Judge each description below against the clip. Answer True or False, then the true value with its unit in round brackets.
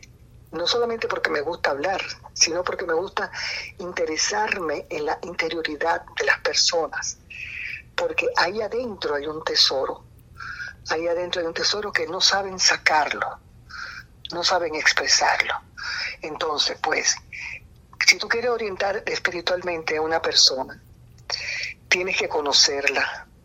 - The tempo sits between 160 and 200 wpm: False (125 wpm)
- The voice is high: True (205 Hz)